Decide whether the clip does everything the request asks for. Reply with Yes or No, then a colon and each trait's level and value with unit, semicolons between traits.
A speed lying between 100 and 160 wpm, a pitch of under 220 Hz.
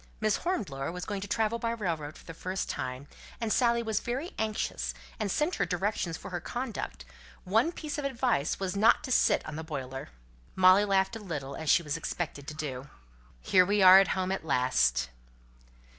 No: average, 195 wpm; high, 190 Hz